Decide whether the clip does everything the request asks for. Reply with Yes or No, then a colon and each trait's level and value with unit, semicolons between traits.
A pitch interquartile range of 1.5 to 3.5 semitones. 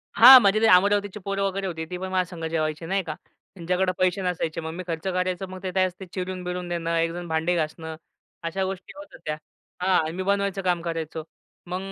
Yes: narrow, 2.5 semitones